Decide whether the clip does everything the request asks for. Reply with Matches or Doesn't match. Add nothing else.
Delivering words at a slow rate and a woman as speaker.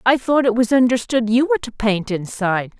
Doesn't match